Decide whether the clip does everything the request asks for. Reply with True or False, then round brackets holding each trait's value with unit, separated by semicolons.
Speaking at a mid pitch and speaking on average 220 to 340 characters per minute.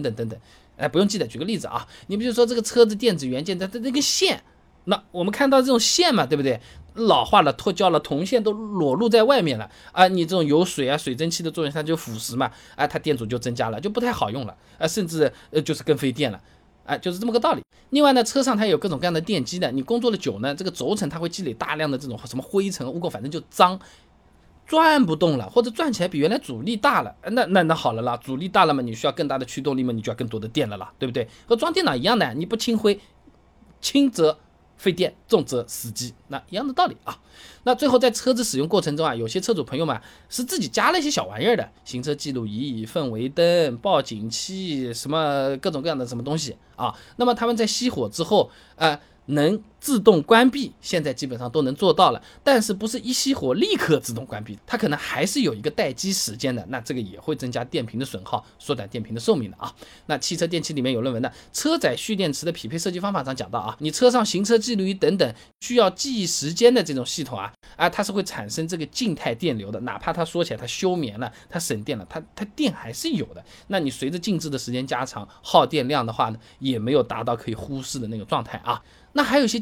False (165 Hz; 360 characters per minute)